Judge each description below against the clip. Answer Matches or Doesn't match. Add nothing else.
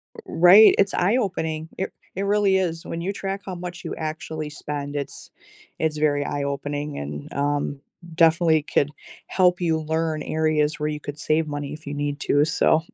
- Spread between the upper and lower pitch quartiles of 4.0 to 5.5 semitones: Doesn't match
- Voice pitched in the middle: Matches